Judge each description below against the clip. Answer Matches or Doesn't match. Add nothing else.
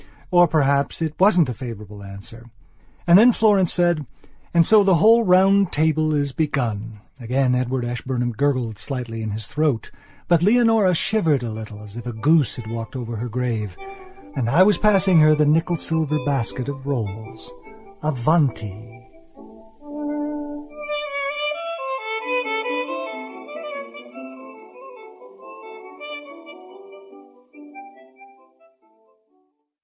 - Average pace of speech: Doesn't match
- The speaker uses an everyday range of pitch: Doesn't match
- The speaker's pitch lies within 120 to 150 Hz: Matches